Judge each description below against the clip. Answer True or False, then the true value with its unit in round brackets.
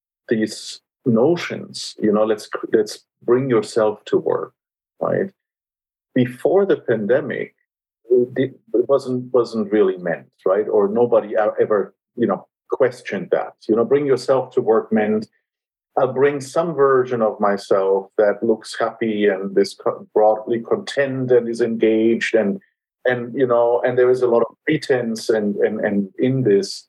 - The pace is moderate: True (145 wpm)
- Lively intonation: True (6.1 semitones)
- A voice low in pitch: True (125 Hz)